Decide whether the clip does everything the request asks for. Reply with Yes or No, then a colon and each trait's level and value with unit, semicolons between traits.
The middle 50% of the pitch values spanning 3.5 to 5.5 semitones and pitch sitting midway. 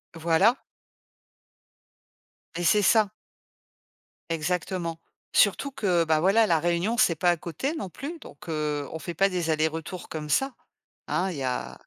Yes: average, 3.8 semitones; medium, 175 Hz